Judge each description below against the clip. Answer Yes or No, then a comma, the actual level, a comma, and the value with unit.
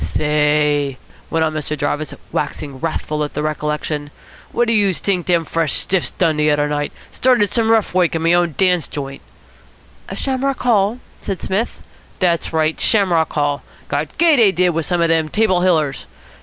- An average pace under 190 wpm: Yes, average, 175 wpm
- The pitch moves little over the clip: No, average, 4.3 semitones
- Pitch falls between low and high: Yes, medium, 165 Hz